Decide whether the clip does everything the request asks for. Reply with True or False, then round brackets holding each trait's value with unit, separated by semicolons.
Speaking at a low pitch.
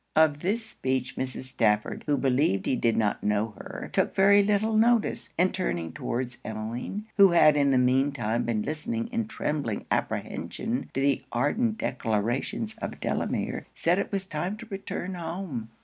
False (145 Hz)